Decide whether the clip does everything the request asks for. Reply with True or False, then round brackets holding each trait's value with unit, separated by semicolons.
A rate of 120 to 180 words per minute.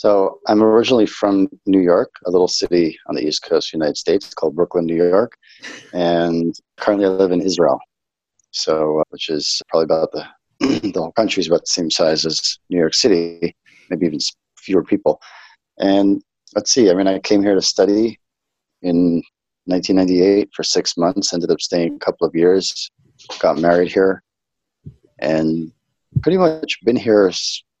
True (170 wpm)